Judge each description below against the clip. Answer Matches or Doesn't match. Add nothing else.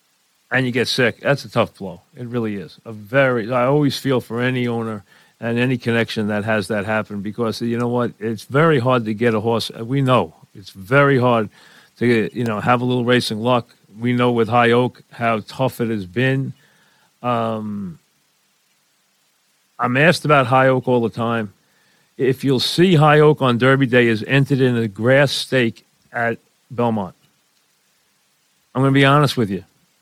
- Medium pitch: Doesn't match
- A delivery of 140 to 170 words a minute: Doesn't match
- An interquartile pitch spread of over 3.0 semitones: Doesn't match